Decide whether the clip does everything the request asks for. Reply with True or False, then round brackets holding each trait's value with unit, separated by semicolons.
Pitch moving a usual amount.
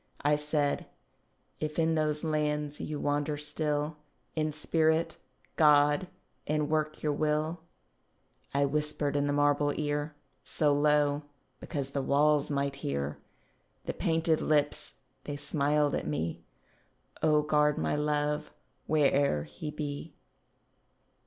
False (1.0 semitones)